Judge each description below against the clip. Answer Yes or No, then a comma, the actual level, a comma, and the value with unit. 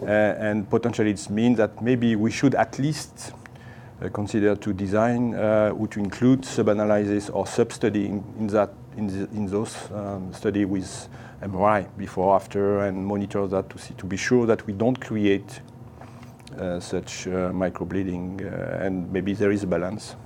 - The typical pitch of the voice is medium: No, low, 105 Hz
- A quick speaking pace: No, average, 165 wpm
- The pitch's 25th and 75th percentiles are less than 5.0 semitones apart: Yes, average, 3.0 semitones